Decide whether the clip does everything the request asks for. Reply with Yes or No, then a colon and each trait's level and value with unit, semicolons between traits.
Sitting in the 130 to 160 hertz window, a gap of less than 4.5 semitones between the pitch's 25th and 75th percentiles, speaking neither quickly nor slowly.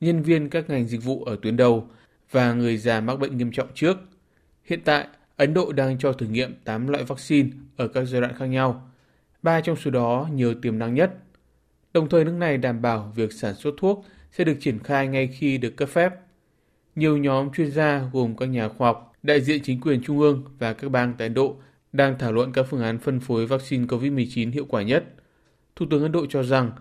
Yes: low, 135 Hz; average, 3.5 semitones; average, 225 wpm